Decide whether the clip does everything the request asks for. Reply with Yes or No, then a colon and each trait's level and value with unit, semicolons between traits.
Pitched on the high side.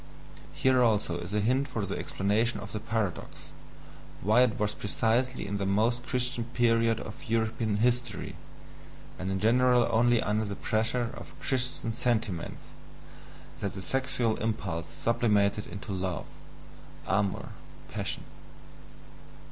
No: low, 110 Hz